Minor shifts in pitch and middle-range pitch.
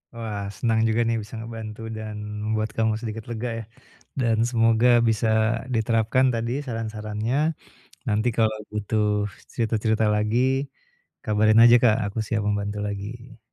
No: narrow, 1.4 semitones; low, 110 Hz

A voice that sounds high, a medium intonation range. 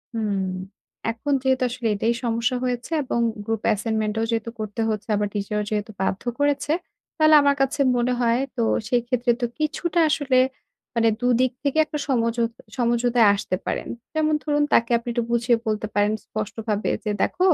Yes: high, 235 Hz; average, 3.4 semitones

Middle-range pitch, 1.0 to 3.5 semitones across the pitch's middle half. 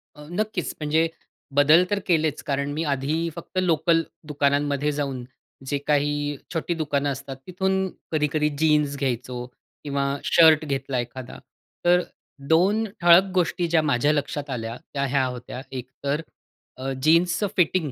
Yes: medium, 150 Hz; average, 3.1 semitones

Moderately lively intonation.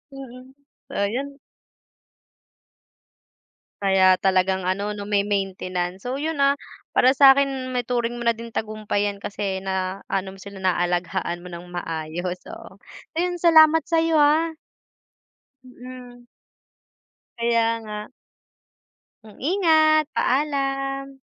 No: wide, 6.2 semitones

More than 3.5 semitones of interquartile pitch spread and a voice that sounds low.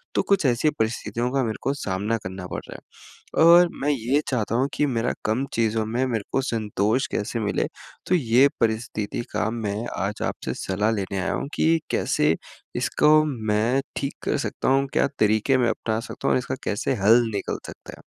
Yes: average, 4.0 semitones; low, 115 Hz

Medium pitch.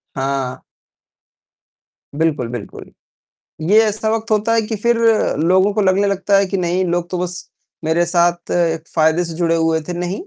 Yes: medium, 175 Hz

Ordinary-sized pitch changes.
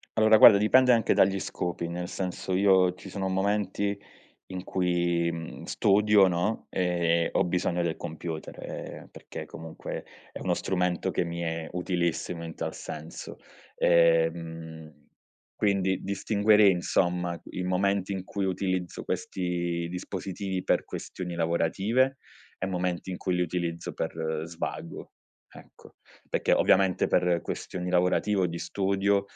No: narrow, 2.2 semitones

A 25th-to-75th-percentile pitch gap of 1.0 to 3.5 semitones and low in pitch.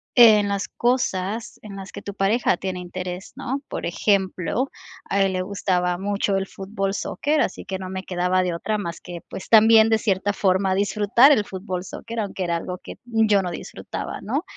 No: average, 2.7 semitones; high, 195 Hz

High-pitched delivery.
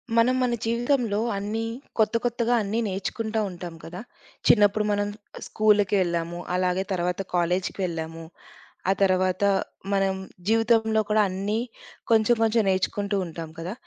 Yes: high, 200 Hz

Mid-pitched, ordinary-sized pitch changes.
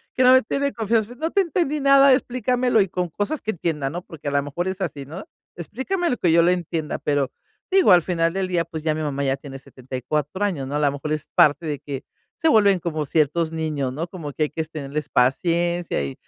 No: medium, 165 Hz; wide, 6.0 semitones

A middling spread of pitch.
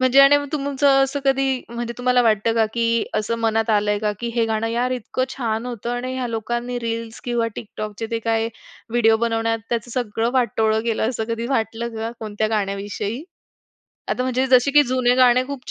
No: narrow, 2.1 semitones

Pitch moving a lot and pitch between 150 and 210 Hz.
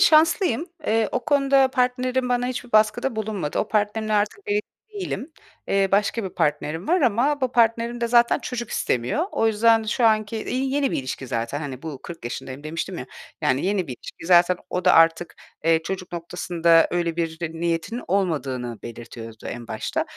Yes: wide, 7.1 semitones; high, 205 Hz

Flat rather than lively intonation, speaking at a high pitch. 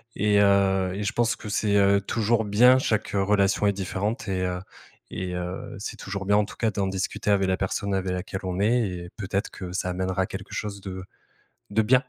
No: narrow, 1.9 semitones; low, 100 Hz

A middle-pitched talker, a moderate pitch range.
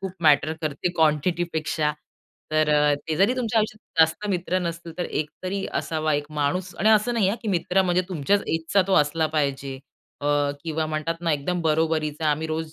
Yes: medium, 160 Hz; average, 3.2 semitones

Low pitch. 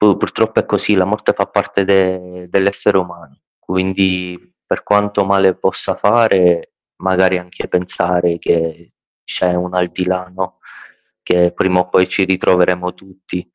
Yes: very low, 90 Hz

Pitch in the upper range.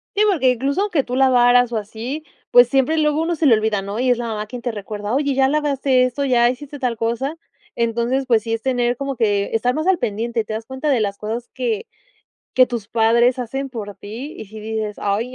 Yes: high, 245 Hz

